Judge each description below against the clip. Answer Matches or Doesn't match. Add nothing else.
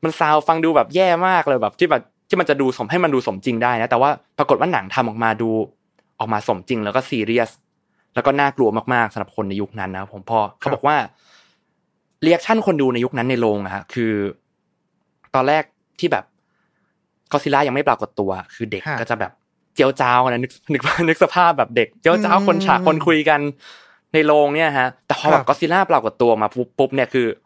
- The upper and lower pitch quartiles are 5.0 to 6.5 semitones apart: Matches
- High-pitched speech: Doesn't match